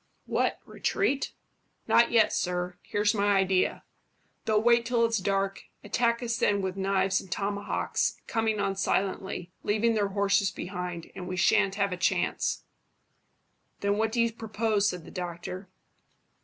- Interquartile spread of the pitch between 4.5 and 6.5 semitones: No, average, 2.7 semitones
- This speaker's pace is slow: No, average, 150 wpm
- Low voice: No, high, 200 Hz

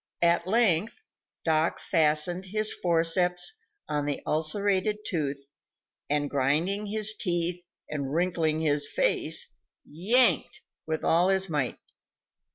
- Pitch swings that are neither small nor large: Yes, average, 3.9 semitones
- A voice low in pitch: No, medium, 170 Hz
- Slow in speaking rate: Yes, slow, 110 wpm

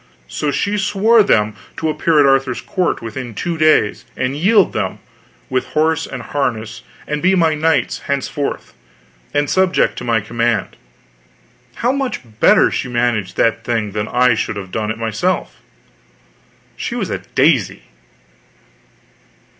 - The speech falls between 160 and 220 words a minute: No, average, 145 wpm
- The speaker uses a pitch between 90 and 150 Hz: Yes, low, 135 Hz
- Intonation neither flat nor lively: No, wide, 6.2 semitones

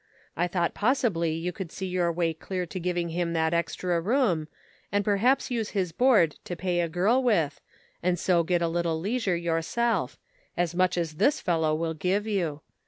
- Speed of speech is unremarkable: Yes, average, 190 wpm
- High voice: No, medium, 175 Hz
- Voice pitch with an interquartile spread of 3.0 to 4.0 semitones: Yes, average, 3.3 semitones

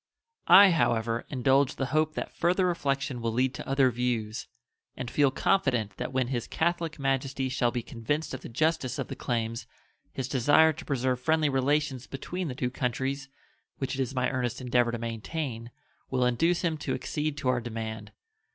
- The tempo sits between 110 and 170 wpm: No, average, 180 wpm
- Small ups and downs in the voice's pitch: No, average, 3.5 semitones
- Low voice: Yes, low, 130 Hz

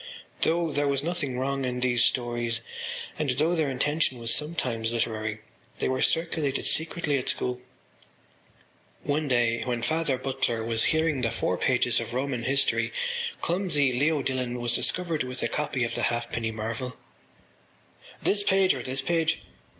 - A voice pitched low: Yes, low, 130 Hz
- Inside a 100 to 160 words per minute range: Yes, average, 155 wpm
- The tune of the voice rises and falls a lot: No, average, 4.2 semitones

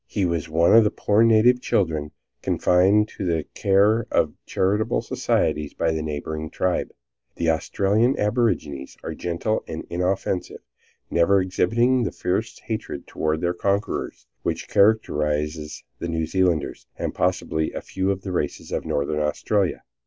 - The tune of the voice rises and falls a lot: No, average, 4.8 semitones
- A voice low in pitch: Yes, very low, 90 Hz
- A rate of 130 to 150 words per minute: Yes, average, 145 wpm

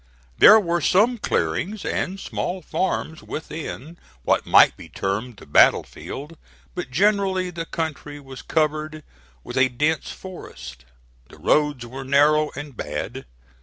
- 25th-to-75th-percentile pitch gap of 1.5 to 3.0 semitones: No, average, 5.1 semitones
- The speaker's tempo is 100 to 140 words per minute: Yes, slow, 135 wpm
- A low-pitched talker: No, medium, 155 Hz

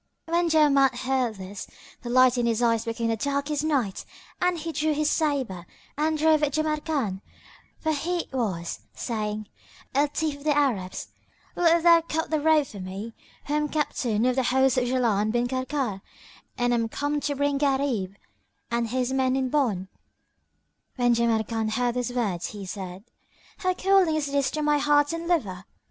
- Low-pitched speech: No, very high, 265 Hz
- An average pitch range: Yes, average, 4.7 semitones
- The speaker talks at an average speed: Yes, average, 175 wpm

